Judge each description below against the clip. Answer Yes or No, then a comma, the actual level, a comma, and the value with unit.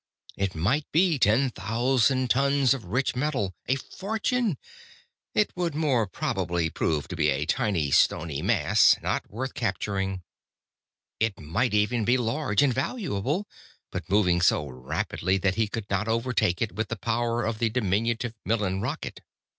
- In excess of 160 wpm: No, average, 155 wpm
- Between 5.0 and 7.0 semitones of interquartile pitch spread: Yes, average, 5.3 semitones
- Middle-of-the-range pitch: No, low, 115 Hz